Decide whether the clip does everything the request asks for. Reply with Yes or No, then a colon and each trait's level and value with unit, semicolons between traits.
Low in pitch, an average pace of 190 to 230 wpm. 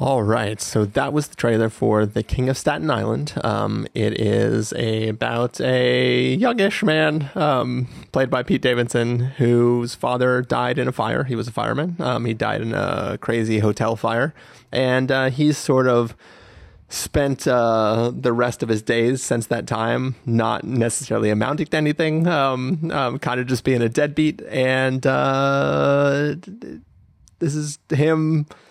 No: low, 125 Hz; average, 160 wpm